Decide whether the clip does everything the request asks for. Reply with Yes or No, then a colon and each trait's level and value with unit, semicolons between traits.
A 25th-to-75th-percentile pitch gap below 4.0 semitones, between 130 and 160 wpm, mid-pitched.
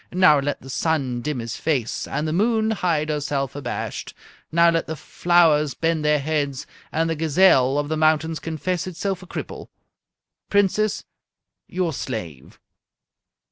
Yes: average, 3.3 semitones; average, 145 wpm; medium, 155 Hz